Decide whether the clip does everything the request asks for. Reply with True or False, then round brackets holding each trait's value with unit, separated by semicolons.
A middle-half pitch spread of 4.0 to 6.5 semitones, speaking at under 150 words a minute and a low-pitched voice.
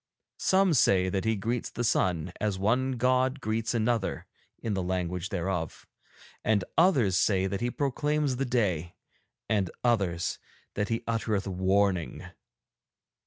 True (4.5 semitones; 135 wpm; 105 Hz)